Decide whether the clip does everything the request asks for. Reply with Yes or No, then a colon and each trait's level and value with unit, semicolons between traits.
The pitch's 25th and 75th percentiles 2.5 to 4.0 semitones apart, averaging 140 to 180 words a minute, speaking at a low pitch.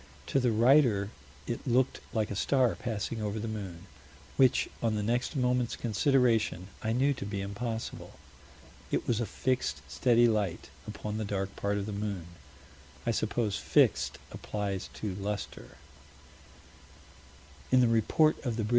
Yes: average, 3.3 semitones; average, 155 wpm; low, 110 Hz